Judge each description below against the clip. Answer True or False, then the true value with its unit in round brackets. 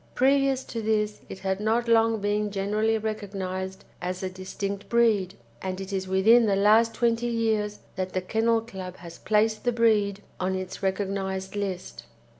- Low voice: False (205 Hz)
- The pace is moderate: True (165 wpm)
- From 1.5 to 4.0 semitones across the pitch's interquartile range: True (2.8 semitones)